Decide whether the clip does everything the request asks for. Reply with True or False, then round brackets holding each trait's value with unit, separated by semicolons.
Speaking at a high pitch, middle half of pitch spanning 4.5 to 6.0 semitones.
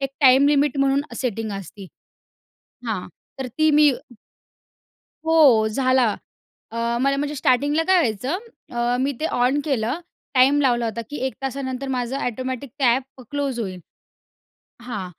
False (260 Hz; 2.9 semitones)